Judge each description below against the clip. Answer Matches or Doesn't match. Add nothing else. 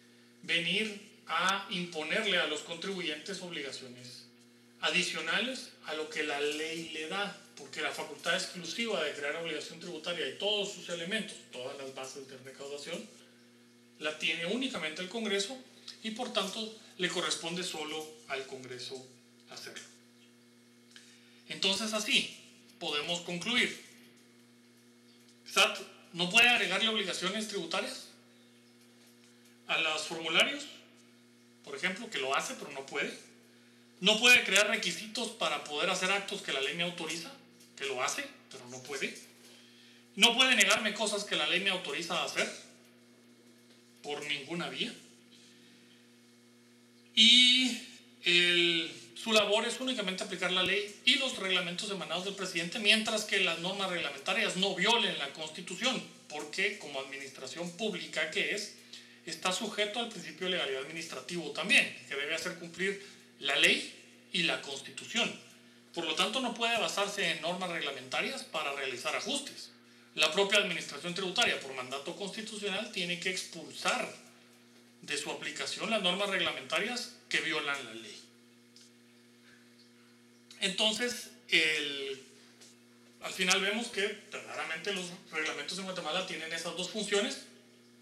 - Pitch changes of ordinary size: Doesn't match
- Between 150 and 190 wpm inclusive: Doesn't match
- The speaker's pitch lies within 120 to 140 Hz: Doesn't match